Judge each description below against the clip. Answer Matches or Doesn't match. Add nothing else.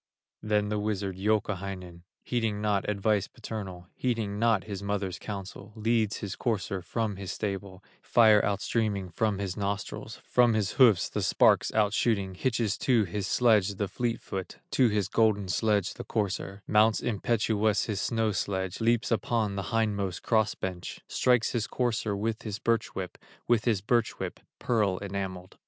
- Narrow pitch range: Matches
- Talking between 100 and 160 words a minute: Matches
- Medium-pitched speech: Doesn't match